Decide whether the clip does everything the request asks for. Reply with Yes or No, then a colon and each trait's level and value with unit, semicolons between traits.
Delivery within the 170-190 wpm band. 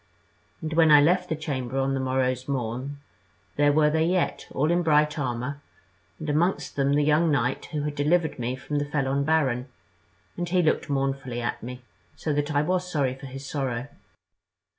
Yes: average, 185 wpm